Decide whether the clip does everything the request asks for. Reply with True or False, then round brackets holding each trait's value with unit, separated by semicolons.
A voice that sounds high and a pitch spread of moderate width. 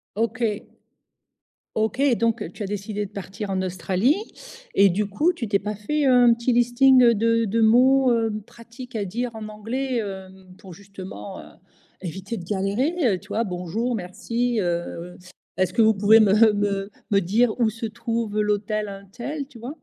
True (215 Hz; 3.2 semitones)